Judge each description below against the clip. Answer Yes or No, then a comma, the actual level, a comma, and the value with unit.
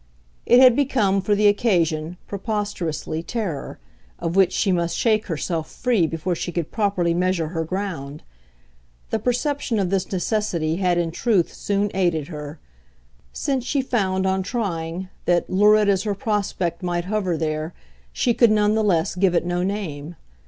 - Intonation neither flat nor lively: Yes, average, 3.8 semitones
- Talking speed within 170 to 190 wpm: No, average, 160 wpm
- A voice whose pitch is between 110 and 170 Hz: No, medium, 185 Hz